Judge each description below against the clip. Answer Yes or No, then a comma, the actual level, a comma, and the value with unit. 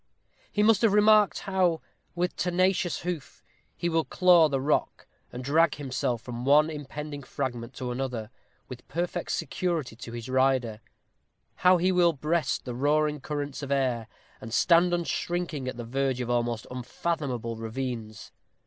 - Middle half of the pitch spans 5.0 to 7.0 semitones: Yes, wide, 5.6 semitones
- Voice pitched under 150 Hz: Yes, medium, 140 Hz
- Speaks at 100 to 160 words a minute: Yes, average, 150 wpm